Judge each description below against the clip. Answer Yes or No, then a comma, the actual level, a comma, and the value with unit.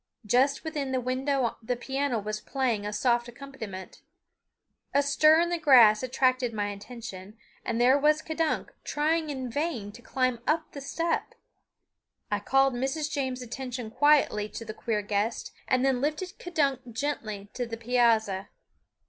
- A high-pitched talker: Yes, very high, 255 Hz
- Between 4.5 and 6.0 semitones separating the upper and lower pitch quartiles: No, average, 4.0 semitones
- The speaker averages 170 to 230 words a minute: No, average, 155 wpm